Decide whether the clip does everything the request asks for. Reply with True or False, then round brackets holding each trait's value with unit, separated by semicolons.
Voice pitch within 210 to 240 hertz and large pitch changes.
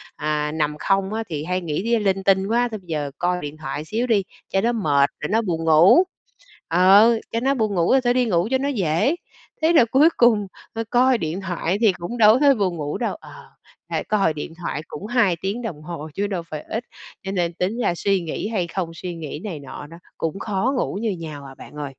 False (190 Hz; 5.8 semitones)